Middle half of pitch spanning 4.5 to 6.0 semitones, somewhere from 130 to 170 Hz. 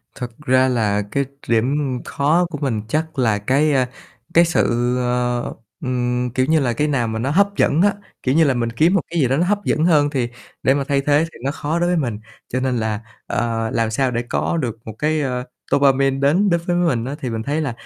No: average, 4.1 semitones; low, 135 Hz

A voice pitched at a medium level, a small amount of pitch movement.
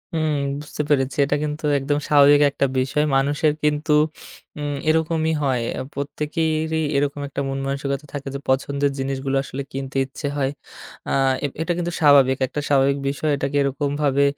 Yes: medium, 145 Hz; narrow, 1.6 semitones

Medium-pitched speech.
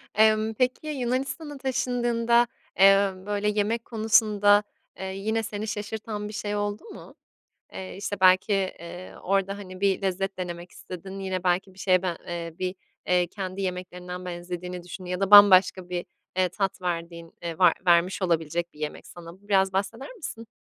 No: high, 195 Hz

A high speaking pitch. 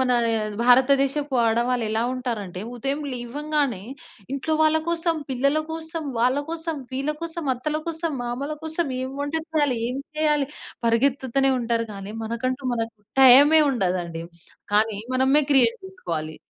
Yes: very high, 265 Hz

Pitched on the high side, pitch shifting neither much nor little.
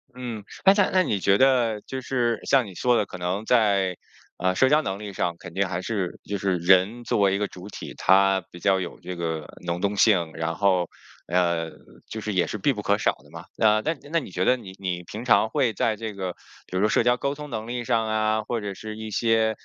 No: low, 105 Hz; average, 3.8 semitones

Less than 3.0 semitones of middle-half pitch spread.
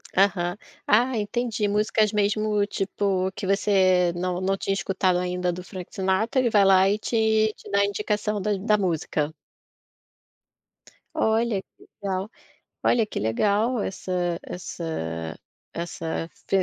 Yes: narrow, 2.6 semitones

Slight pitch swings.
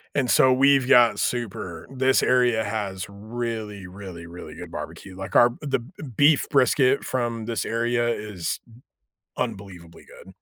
No: average, 4.4 semitones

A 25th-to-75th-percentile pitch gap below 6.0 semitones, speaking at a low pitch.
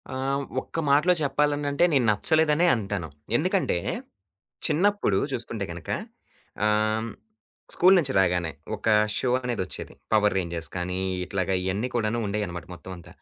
No: wide, 7.3 semitones; low, 110 Hz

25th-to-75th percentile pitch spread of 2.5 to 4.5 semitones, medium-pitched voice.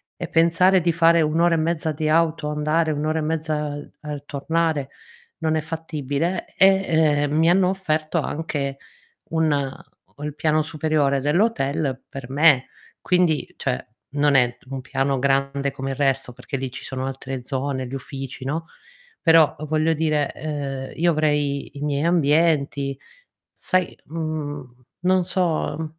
Yes: average, 2.8 semitones; medium, 150 Hz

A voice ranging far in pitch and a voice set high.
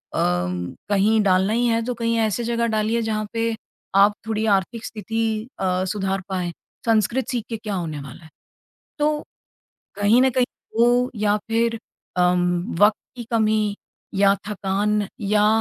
No: average, 2.9 semitones; high, 215 Hz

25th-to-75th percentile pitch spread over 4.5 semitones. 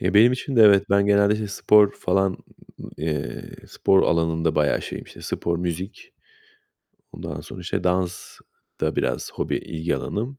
No: average, 3.3 semitones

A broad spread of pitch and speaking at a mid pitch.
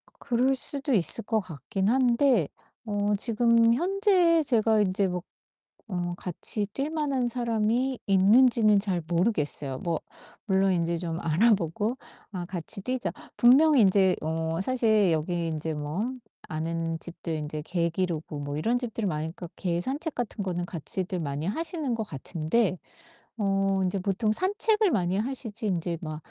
No: wide, 5.9 semitones; high, 195 Hz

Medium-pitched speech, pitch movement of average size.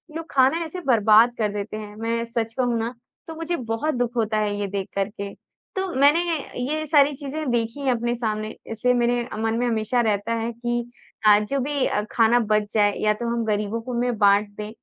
No: high, 230 Hz; average, 3.0 semitones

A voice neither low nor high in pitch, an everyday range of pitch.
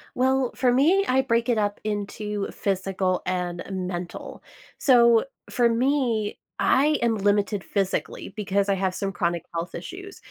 No: high, 210 Hz; average, 4.7 semitones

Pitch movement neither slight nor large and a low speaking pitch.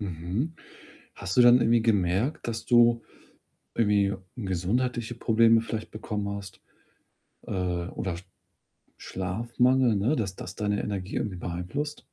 Yes: average, 4.0 semitones; low, 110 Hz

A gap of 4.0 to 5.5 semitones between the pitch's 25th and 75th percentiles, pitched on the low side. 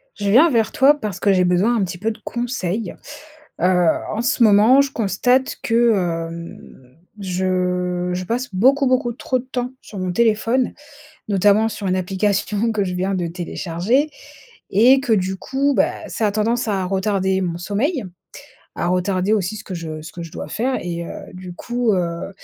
No: average, 4.6 semitones; high, 200 Hz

